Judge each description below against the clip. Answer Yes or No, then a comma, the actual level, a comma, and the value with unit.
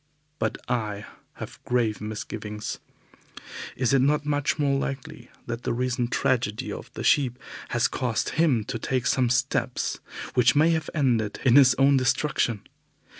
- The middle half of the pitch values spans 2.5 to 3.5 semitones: Yes, average, 2.9 semitones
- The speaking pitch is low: Yes, low, 125 Hz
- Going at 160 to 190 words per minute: No, average, 150 wpm